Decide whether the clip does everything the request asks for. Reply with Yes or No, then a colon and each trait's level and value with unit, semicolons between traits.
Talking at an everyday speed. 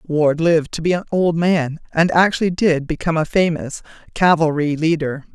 Yes: average, 170 wpm